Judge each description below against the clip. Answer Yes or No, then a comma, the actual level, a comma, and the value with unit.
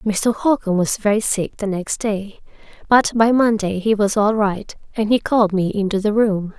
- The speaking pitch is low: No, high, 210 Hz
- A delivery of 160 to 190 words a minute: No, average, 200 wpm